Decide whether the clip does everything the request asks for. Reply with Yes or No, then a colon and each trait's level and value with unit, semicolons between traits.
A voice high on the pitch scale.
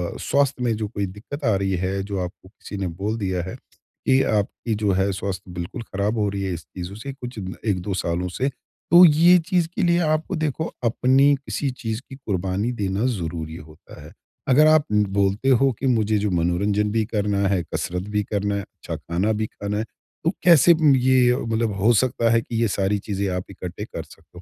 No: low, 105 Hz